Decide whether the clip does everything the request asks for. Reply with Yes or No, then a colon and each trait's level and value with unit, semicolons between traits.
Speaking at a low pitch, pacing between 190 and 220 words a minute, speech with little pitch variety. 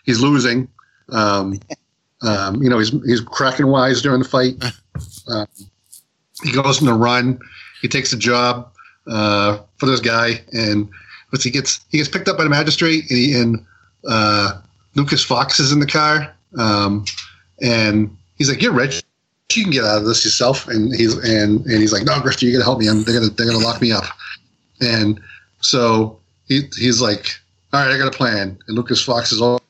No: low, 120 Hz; average, 200 wpm; average, 3.7 semitones